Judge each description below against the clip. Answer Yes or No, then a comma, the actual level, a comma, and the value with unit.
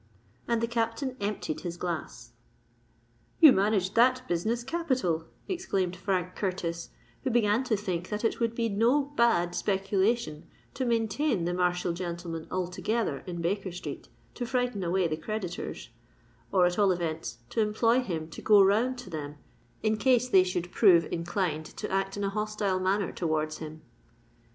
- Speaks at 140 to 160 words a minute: Yes, average, 155 wpm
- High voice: Yes, high, 195 Hz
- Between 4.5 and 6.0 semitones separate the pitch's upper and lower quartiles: Yes, average, 4.8 semitones